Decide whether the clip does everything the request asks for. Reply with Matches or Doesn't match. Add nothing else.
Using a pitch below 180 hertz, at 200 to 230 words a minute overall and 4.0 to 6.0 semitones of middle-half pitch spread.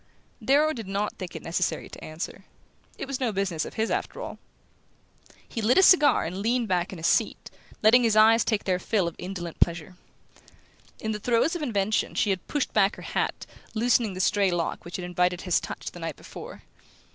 Doesn't match